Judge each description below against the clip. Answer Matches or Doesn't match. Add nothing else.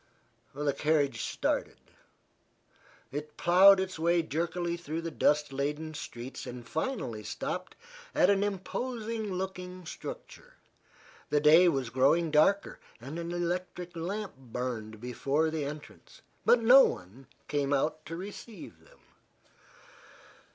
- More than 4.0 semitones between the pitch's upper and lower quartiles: Matches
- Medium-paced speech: Doesn't match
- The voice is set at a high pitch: Doesn't match